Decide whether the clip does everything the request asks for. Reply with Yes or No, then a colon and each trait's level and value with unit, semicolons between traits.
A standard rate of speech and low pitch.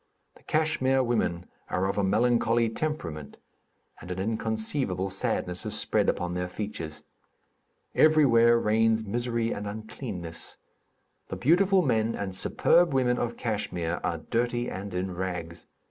No: slow, 130 wpm; low, 110 Hz